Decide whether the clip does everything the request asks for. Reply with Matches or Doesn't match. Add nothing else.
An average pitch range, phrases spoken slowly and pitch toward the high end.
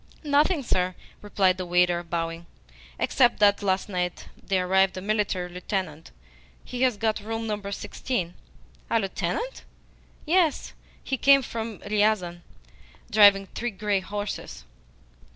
Matches